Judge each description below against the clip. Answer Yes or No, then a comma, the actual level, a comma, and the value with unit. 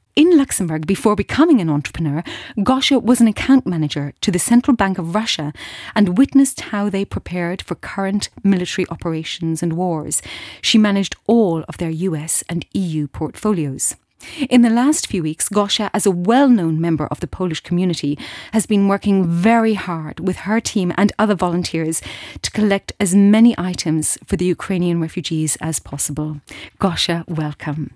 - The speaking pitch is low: No, medium, 185 Hz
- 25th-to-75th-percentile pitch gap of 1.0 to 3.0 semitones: No, average, 4.7 semitones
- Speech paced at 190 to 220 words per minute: No, average, 165 wpm